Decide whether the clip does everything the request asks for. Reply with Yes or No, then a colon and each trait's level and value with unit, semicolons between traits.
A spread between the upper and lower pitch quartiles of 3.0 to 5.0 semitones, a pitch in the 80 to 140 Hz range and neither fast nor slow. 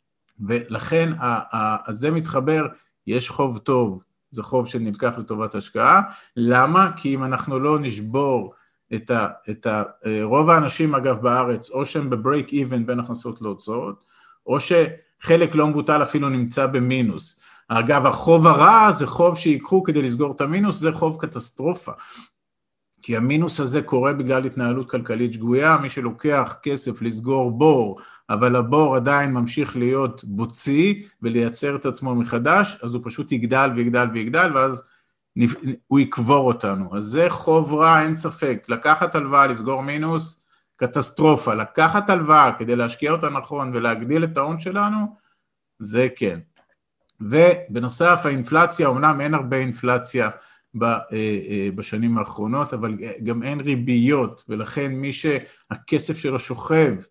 Yes: average, 4.4 semitones; low, 135 Hz; average, 130 wpm